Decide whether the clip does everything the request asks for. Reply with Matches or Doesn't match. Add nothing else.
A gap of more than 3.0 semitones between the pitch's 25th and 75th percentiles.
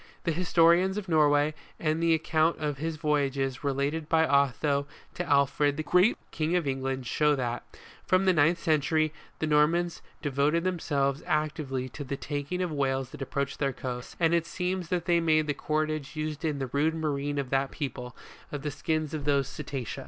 Doesn't match